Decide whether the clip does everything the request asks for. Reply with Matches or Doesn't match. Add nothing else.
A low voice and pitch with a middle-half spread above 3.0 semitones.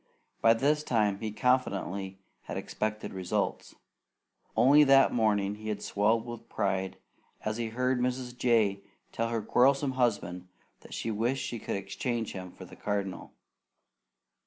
Matches